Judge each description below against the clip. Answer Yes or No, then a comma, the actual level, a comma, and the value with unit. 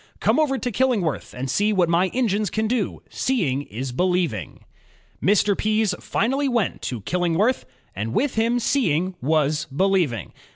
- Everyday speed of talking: Yes, average, 150 wpm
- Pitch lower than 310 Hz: Yes, high, 190 Hz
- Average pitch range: No, wide, 7.1 semitones